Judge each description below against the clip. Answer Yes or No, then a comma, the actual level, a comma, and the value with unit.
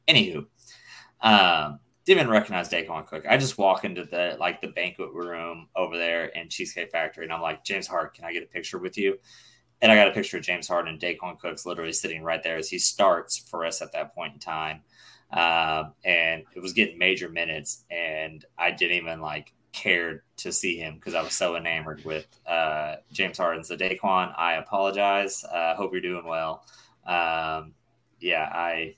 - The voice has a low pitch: Yes, very low, 85 Hz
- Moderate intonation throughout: No, narrow, 2.3 semitones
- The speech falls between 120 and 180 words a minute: No, average, 200 wpm